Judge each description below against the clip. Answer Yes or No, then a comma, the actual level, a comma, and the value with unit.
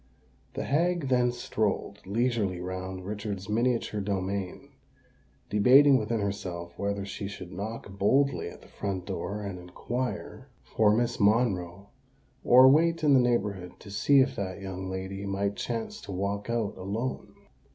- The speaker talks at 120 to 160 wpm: Yes, average, 145 wpm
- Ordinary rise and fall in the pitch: Yes, average, 4.0 semitones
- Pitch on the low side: Yes, low, 100 Hz